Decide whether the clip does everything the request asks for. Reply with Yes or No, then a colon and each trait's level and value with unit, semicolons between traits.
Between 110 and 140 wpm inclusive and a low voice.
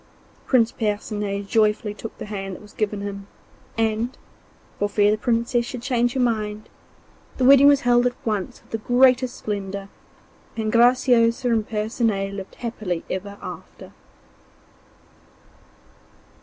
No: slow, 135 wpm; high, 220 Hz